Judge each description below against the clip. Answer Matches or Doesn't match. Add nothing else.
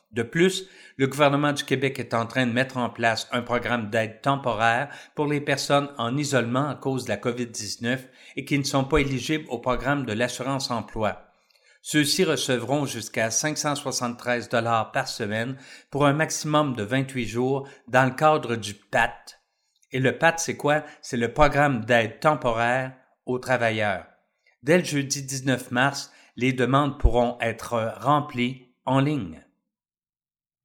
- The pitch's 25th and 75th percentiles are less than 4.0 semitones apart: Matches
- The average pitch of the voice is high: Doesn't match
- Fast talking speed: Doesn't match